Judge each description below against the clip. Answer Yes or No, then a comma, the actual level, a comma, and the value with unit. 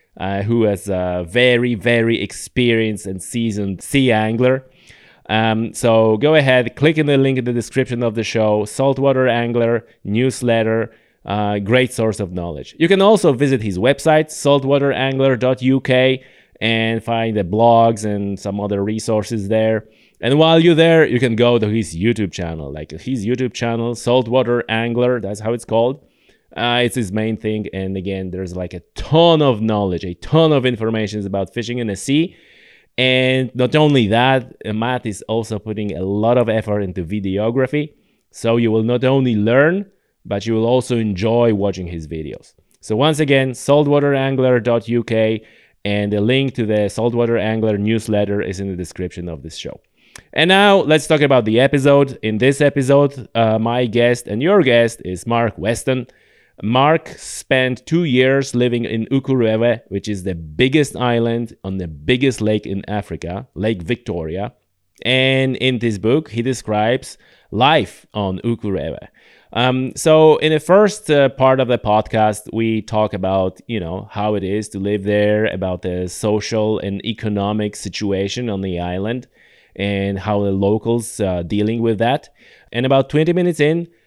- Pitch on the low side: Yes, low, 115 Hz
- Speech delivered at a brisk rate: No, average, 165 wpm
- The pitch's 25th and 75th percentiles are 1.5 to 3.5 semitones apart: No, average, 3.9 semitones